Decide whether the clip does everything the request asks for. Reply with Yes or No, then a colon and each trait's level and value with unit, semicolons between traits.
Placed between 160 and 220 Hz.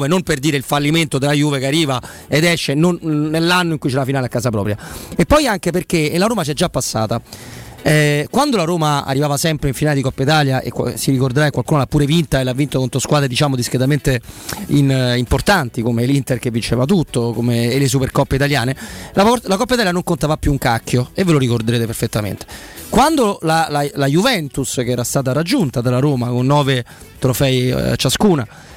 No: medium, 140 Hz